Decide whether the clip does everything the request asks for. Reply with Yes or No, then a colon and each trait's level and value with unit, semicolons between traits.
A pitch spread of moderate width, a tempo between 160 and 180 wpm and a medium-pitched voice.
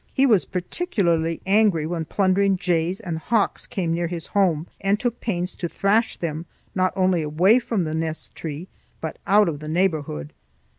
Yes: average, 3.5 semitones; average, 170 wpm; medium, 180 Hz